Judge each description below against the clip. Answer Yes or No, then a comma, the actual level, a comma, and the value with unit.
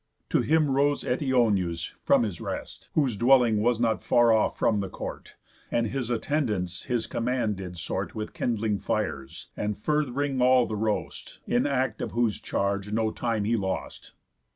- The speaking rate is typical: Yes, average, 170 wpm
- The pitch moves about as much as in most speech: Yes, average, 3.6 semitones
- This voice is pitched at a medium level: No, low, 115 Hz